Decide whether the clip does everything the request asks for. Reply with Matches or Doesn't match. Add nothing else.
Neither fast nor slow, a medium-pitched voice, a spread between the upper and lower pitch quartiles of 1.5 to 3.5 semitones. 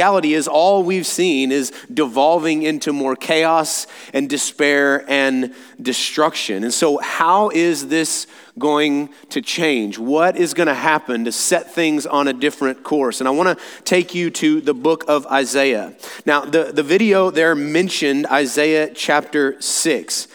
Matches